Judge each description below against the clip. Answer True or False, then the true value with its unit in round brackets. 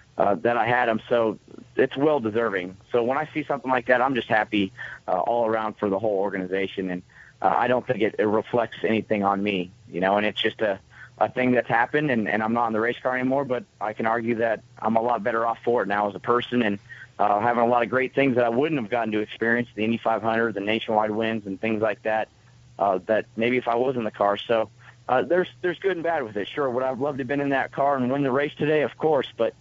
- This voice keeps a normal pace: False (270 wpm)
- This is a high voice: False (115 Hz)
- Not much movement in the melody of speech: False (3.0 semitones)